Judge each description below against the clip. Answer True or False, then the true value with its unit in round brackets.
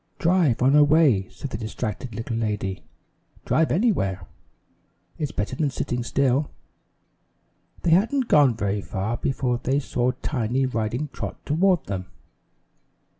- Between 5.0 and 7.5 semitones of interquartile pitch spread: True (5.5 semitones)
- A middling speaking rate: False (130 wpm)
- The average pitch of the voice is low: True (125 Hz)